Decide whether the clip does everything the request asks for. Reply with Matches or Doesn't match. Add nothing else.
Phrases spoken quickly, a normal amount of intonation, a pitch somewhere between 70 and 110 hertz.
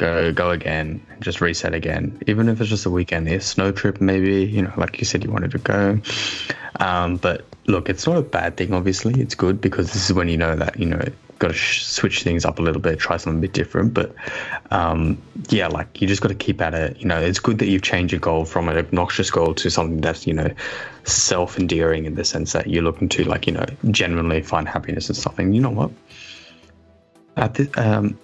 Matches